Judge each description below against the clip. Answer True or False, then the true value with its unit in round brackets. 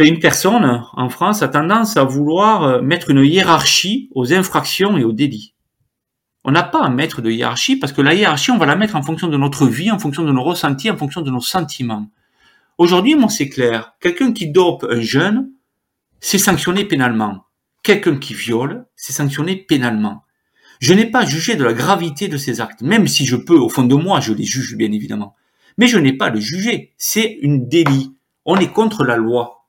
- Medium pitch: True (150 Hz)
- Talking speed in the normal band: True (205 wpm)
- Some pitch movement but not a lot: False (7.0 semitones)